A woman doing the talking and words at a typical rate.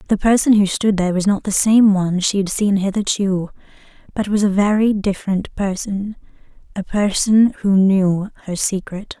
Yes: female; average, 165 wpm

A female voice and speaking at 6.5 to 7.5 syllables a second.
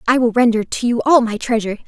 Yes: female; 6.7 syllables/s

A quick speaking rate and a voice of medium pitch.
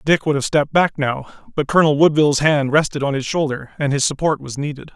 Yes: fast, 230 wpm; medium, 145 Hz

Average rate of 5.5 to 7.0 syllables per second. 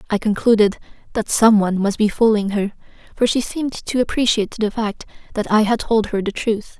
Yes: 5.6 syllables/s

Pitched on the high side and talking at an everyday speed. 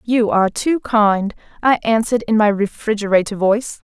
Yes: high, 220 Hz; average, 155 wpm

